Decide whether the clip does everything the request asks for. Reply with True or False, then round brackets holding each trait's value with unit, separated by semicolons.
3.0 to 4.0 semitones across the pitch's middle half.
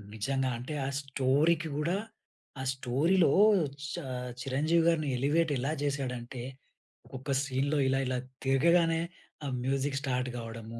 True (3.3 semitones)